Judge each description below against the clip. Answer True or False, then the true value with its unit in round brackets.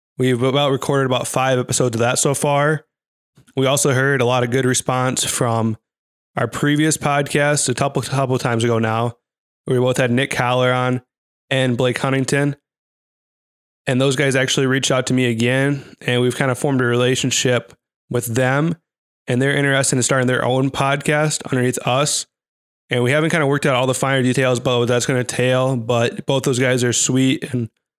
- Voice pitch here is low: True (130 Hz)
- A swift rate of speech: False (190 wpm)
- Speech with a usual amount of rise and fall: False (1.9 semitones)